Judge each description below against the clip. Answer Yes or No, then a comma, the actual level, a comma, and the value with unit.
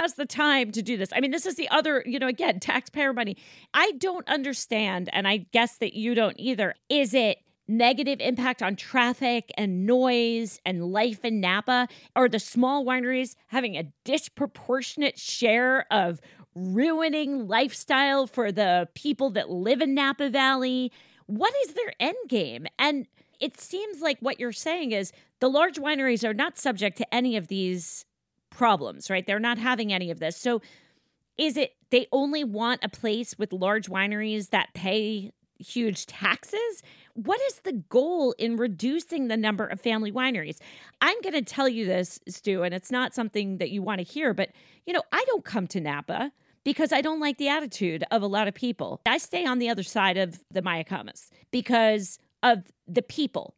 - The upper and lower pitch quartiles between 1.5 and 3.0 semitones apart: No, average, 5.2 semitones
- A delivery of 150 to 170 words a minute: No, average, 185 wpm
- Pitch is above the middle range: Yes, high, 245 Hz